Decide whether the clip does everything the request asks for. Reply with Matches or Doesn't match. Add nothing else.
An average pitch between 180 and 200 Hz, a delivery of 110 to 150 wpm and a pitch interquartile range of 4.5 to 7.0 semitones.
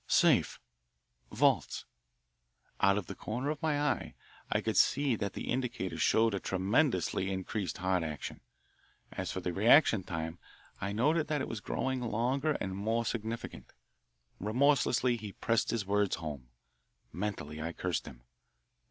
Doesn't match